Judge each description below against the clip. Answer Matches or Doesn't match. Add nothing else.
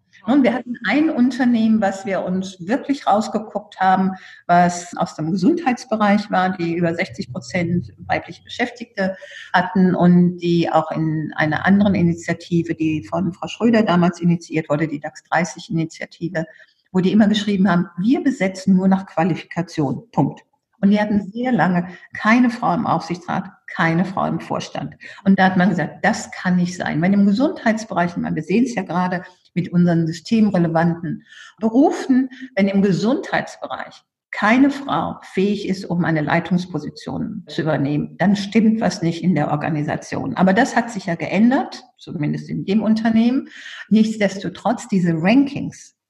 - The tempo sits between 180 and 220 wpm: Doesn't match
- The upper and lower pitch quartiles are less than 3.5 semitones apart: Doesn't match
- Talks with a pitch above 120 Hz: Matches